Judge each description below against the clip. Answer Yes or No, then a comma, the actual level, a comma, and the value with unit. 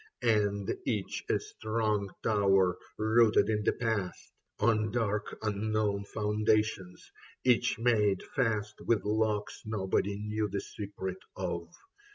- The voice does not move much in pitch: Yes, narrow, 1.6 semitones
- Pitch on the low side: Yes, low, 105 Hz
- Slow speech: Yes, slow, 115 wpm